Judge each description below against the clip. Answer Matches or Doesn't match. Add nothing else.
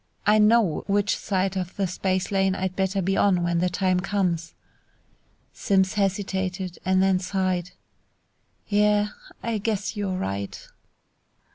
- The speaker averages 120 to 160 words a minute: Matches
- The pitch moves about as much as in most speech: Doesn't match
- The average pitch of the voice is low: Doesn't match